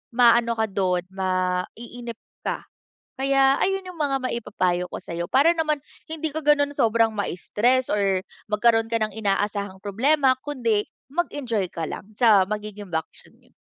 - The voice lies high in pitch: Yes, high, 225 Hz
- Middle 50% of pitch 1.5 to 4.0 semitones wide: No, wide, 5.4 semitones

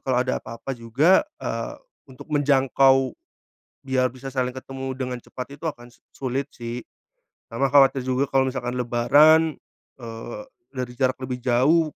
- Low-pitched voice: Yes, low, 130 Hz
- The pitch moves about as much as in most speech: No, narrow, 1.8 semitones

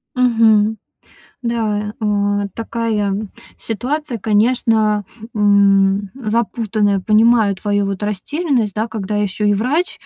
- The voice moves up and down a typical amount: No, narrow, 2.2 semitones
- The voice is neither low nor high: No, high, 210 Hz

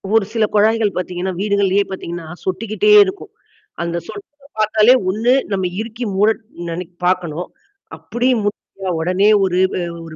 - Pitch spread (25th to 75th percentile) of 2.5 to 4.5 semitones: Yes, average, 3.4 semitones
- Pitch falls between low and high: No, high, 195 Hz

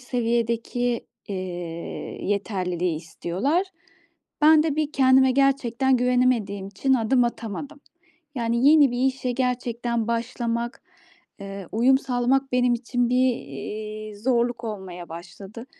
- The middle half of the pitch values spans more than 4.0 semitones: No, average, 3.4 semitones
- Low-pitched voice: No, high, 240 Hz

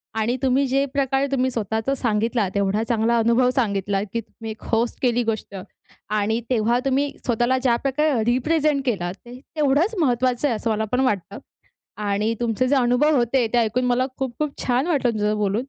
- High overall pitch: Yes, high, 240 Hz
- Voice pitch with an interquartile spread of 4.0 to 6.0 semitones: No, average, 3.3 semitones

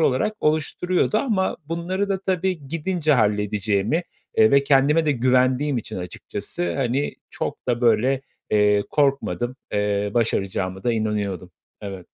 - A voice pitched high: No, low, 130 Hz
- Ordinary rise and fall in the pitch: No, wide, 6.9 semitones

